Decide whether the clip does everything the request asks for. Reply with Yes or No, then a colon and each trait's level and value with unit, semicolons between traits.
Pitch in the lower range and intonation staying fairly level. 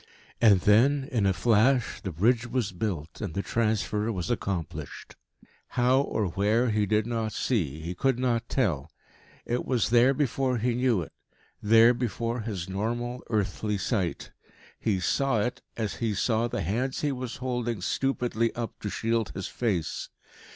No: low, 115 Hz; average, 3.7 semitones